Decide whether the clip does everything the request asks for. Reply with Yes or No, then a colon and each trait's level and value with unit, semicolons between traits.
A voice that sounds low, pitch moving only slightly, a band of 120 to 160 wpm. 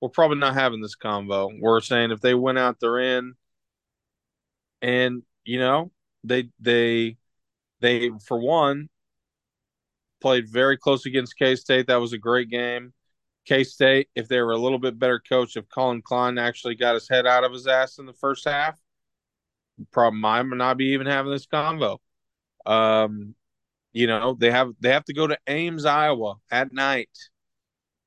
No: low, 125 Hz; narrow, 2.0 semitones; average, 170 wpm